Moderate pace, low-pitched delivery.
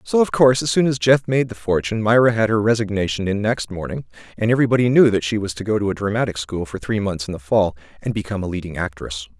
No: fast, 255 wpm; low, 105 Hz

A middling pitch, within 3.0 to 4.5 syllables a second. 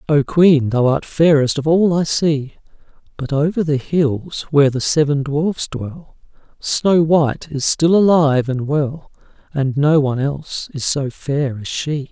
Yes: medium, 145 Hz; 4.2 syllables/s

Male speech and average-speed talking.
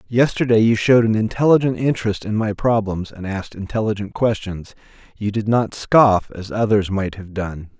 Yes: male; average, 170 wpm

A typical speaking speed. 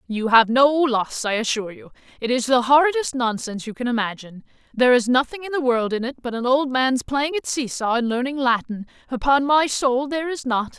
No: fast, 225 wpm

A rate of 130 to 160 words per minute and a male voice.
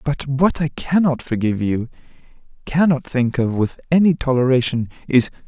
Yes: average, 140 wpm; male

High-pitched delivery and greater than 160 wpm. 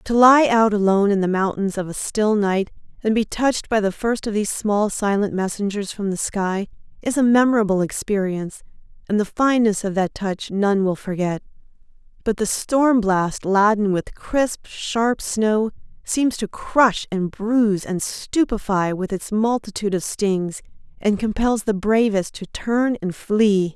Yes: high, 210 Hz; average, 170 wpm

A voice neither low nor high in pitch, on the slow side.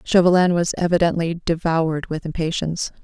Yes: medium, 165 Hz; slow, 120 wpm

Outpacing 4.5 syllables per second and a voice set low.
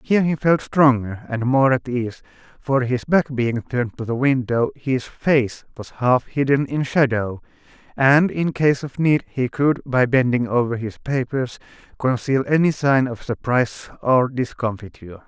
No: 4.4 syllables/s; low, 130 Hz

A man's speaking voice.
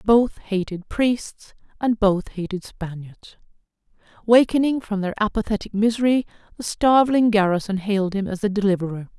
No: female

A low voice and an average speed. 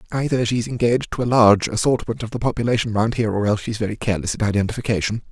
No: low, 110 Hz; fast, 215 wpm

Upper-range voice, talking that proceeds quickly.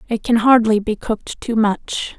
No: high, 225 Hz; average, 190 wpm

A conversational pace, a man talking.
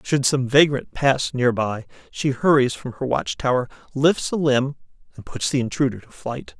Yes: average, 190 wpm; male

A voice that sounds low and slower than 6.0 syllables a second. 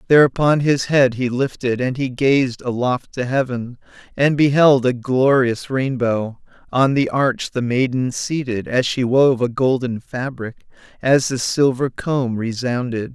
Yes: low, 130 Hz; 4.1 syllables/s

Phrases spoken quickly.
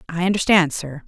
No: average, 165 wpm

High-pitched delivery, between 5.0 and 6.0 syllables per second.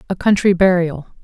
No: medium, 180 Hz; 5.5 syllables/s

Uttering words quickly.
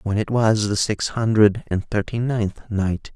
No: average, 190 wpm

